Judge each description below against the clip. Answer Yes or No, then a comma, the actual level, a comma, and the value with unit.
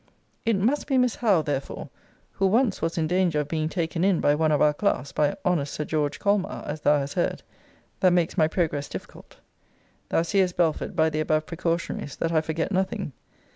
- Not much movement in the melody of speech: No, average, 3.7 semitones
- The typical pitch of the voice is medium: Yes, medium, 165 Hz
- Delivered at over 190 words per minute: Yes, average, 200 wpm